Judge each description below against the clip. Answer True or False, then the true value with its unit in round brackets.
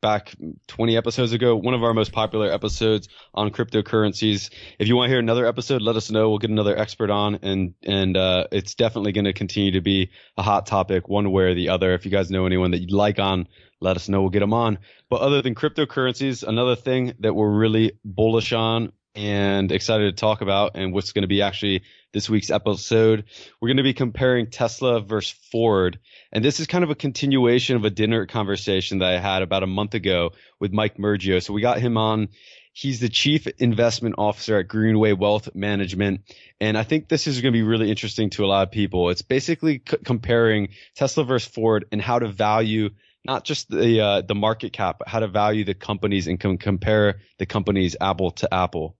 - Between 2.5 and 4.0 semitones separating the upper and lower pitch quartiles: True (2.8 semitones)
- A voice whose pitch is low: True (105 Hz)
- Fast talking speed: True (215 wpm)